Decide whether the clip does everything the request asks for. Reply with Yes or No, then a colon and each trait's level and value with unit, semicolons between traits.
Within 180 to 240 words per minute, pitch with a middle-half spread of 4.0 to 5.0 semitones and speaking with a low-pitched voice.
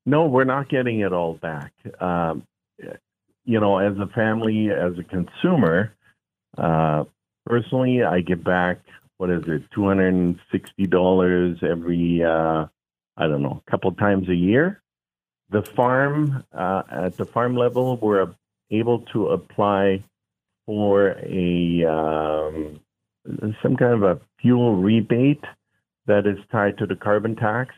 No: slow, 135 wpm; average, 4.6 semitones; low, 100 Hz